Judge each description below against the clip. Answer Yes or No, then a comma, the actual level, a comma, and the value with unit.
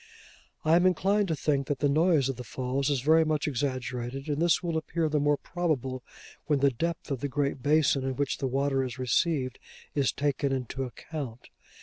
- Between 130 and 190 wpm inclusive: No, average, 200 wpm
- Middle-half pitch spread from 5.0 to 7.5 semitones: No, average, 3.1 semitones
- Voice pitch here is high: No, medium, 140 Hz